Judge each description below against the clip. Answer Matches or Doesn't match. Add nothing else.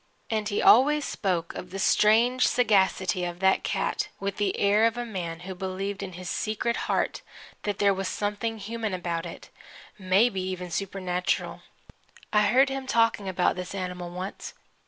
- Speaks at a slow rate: Doesn't match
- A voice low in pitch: Doesn't match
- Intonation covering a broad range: Doesn't match